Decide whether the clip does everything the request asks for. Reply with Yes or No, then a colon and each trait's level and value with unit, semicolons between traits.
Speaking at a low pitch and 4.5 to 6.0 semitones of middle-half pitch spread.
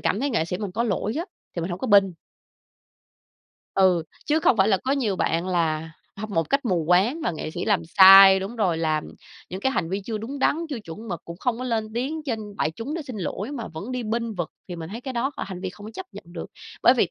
No: high, 205 Hz; average, 5.2 semitones